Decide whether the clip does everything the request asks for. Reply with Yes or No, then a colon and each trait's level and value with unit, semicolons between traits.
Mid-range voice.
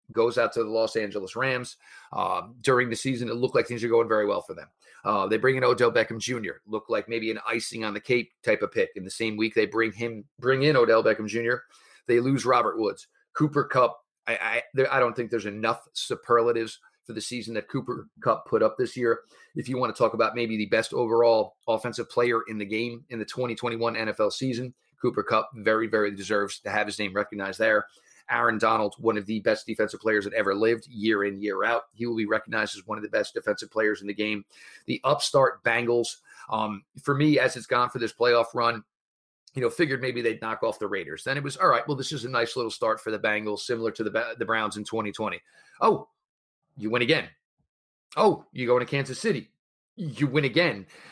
No: low, 115 Hz